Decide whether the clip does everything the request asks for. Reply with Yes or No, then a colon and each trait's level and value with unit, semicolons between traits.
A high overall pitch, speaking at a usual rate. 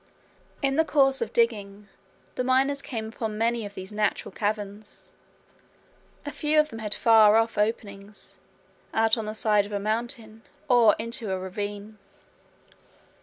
Yes: high, 220 Hz; average, 150 wpm